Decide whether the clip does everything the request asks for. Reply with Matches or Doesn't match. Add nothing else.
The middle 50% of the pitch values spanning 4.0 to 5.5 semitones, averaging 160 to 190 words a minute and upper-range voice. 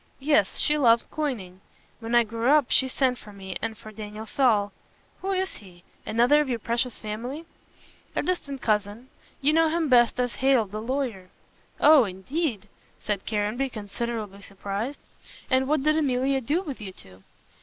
Matches